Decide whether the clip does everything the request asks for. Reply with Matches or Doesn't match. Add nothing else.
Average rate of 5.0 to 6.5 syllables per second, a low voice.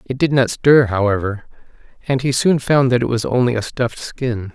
Matches